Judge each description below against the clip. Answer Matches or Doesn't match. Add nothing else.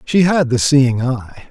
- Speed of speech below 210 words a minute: Matches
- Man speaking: Matches